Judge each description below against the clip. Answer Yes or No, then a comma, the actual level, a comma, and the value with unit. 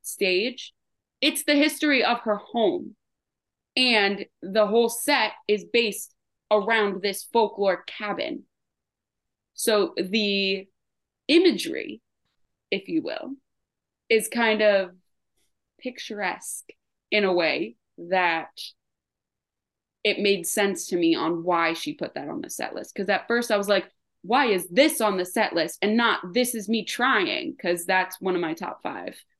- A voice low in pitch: No, high, 215 Hz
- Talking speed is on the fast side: No, average, 145 wpm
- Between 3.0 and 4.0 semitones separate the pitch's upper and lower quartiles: No, average, 5.0 semitones